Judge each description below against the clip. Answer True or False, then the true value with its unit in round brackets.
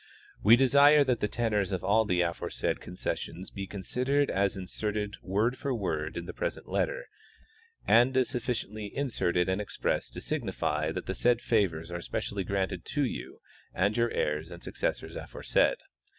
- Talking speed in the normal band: True (165 wpm)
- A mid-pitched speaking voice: False (105 Hz)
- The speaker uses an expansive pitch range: False (4.8 semitones)